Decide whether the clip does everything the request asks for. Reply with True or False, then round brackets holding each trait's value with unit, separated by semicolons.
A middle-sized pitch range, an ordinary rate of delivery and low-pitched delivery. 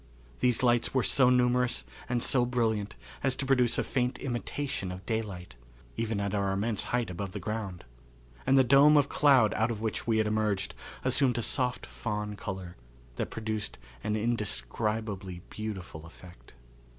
True (3.5 semitones; 160 wpm; 110 Hz)